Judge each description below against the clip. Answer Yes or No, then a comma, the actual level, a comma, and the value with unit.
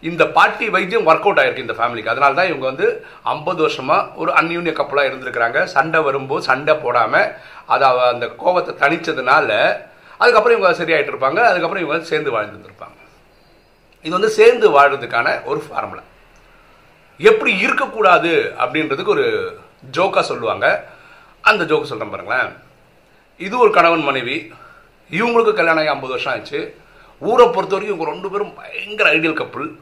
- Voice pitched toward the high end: Yes, high, 205 Hz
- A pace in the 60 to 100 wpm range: No, fast, 130 wpm